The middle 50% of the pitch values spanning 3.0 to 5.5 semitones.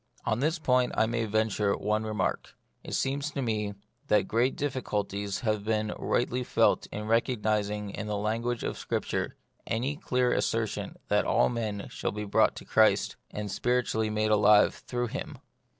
No: narrow, 2.5 semitones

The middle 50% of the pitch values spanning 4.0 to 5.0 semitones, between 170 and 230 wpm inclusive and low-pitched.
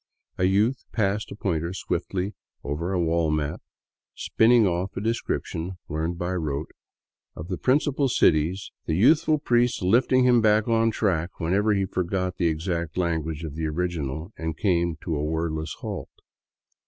No: average, 4.7 semitones; average, 160 wpm; very low, 90 Hz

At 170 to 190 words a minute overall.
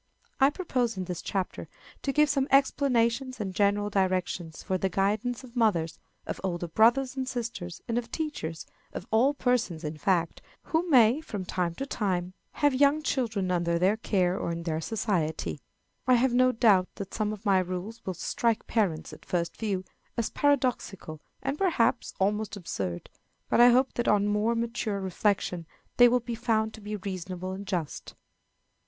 Yes: average, 175 wpm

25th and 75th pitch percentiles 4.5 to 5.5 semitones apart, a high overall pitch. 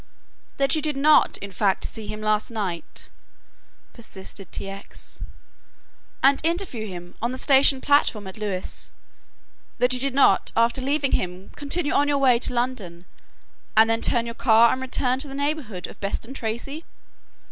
Yes: average, 4.8 semitones; high, 240 Hz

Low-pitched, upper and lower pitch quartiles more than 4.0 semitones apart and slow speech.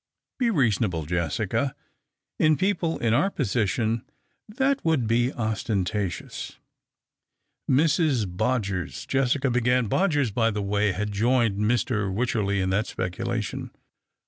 Yes: low, 115 Hz; average, 4.5 semitones; slow, 125 wpm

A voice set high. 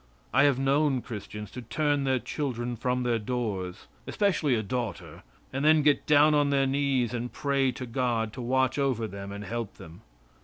No: low, 125 Hz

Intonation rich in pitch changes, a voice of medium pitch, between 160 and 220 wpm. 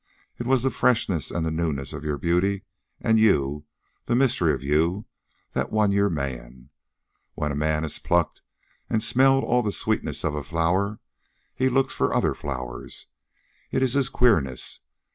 No: wide, 7.2 semitones; very low, 85 Hz; average, 165 wpm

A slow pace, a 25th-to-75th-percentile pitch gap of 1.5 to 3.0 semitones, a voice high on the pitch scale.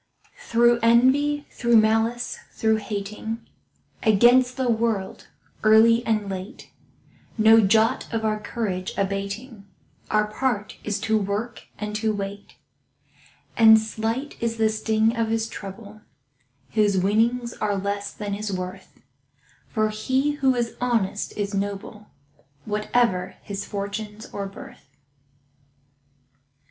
Yes: slow, 120 wpm; narrow, 2.4 semitones; high, 220 Hz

